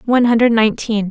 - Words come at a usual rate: Yes, average, 165 wpm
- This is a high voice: Yes, high, 225 Hz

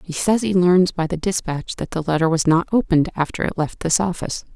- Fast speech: Yes, fast, 235 wpm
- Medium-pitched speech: Yes, medium, 170 Hz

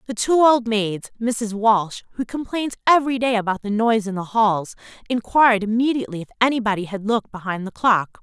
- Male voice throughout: No, female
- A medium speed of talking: Yes, average, 180 wpm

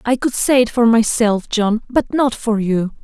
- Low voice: No, high, 230 Hz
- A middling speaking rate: No, fast, 215 wpm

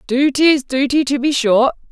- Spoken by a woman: Yes, female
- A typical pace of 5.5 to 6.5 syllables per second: No, 5.0 syllables/s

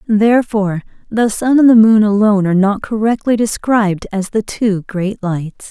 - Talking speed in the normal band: Yes, average, 170 wpm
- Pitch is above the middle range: Yes, high, 210 Hz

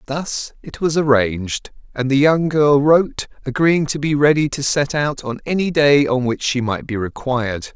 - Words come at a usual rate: Yes, average, 195 wpm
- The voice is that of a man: Yes, male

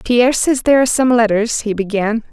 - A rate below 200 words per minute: No, fast, 205 wpm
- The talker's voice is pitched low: No, high, 235 Hz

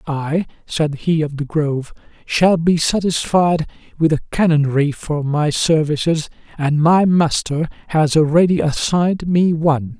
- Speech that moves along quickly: No, average, 140 wpm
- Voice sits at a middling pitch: Yes, medium, 160 Hz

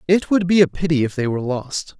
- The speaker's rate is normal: No, fast, 270 wpm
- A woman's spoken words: No, male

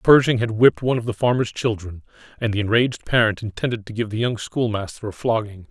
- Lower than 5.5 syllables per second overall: No, 6.3 syllables/s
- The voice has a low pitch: Yes, low, 110 Hz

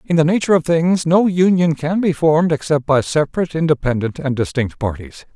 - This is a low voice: No, medium, 155 Hz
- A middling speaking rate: Yes, average, 190 wpm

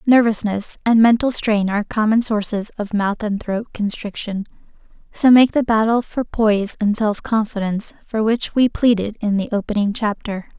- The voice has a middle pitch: No, high, 215 Hz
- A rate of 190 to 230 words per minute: No, average, 165 wpm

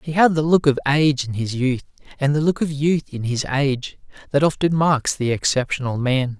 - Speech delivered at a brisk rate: Yes, fast, 215 wpm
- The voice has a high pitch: No, medium, 140 Hz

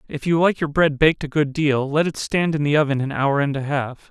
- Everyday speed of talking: No, fast, 290 wpm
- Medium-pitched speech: Yes, medium, 145 Hz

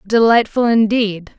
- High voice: Yes, high, 220 Hz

